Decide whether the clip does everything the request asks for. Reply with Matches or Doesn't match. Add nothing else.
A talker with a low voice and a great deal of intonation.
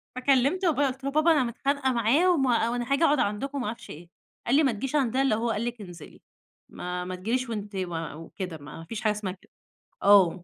Doesn't match